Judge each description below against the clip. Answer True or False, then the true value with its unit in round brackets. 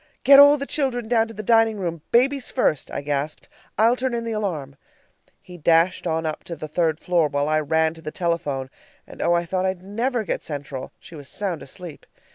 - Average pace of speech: False (215 wpm)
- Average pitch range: False (6.5 semitones)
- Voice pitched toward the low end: False (175 Hz)